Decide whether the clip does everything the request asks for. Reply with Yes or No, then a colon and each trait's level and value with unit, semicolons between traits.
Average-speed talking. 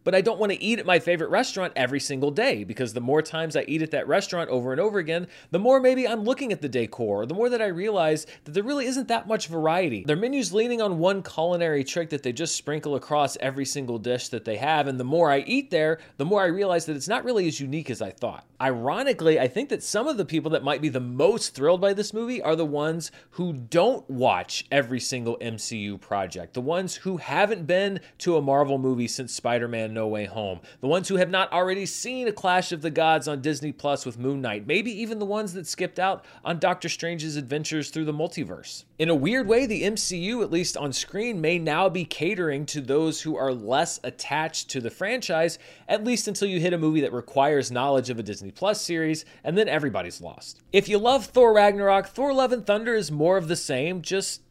No: fast, 235 wpm